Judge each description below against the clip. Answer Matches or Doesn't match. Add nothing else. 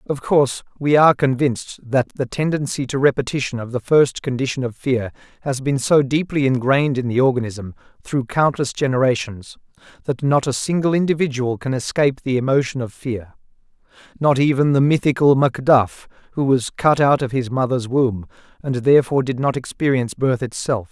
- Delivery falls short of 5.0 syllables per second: Doesn't match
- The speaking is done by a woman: Doesn't match